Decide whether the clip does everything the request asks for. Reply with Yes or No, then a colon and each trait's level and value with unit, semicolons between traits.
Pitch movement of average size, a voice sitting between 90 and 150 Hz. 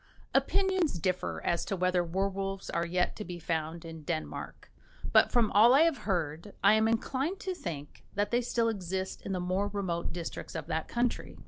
No: average, 5.0 semitones; high, 190 Hz